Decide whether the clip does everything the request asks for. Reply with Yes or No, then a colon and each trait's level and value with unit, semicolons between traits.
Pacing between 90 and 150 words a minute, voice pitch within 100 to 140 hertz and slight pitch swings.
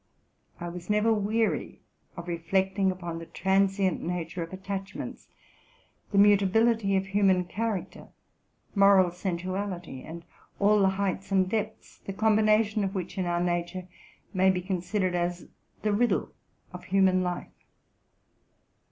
No: slow, 135 wpm; high, 190 Hz; narrow, 2.2 semitones